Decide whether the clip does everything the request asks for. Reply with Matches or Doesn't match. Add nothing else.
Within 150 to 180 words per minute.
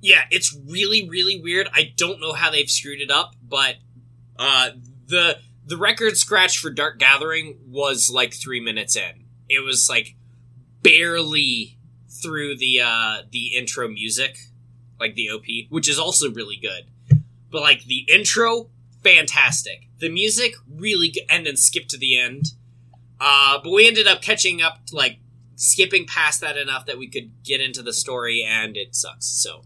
Matches